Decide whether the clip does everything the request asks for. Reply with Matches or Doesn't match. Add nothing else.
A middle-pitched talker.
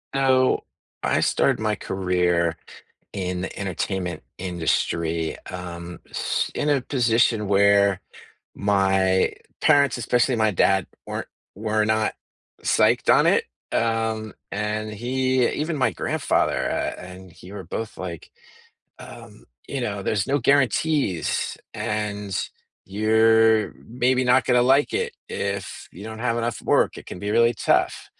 Doesn't match